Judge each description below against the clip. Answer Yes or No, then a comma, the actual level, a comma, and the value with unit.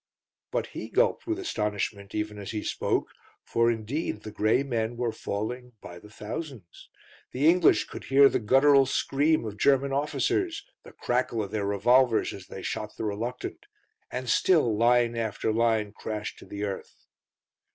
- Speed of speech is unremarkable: Yes, average, 165 wpm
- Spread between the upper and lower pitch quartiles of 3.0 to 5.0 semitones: Yes, average, 4.2 semitones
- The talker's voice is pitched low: Yes, low, 115 Hz